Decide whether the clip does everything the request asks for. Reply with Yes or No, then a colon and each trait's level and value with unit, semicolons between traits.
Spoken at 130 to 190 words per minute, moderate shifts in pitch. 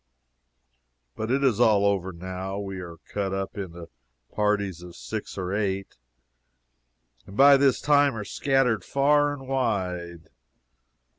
No: slow, 135 wpm; wide, 6.2 semitones